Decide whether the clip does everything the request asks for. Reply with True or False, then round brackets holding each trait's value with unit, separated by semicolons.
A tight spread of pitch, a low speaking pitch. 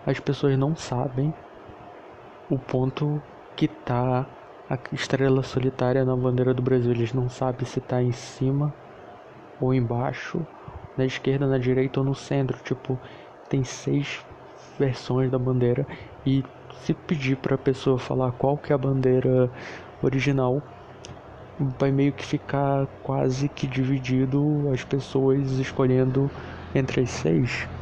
True (1.4 semitones; 130 Hz)